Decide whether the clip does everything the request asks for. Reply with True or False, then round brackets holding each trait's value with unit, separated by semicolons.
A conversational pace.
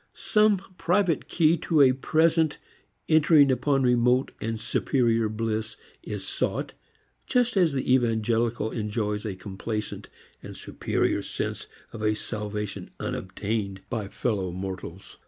False (120 wpm)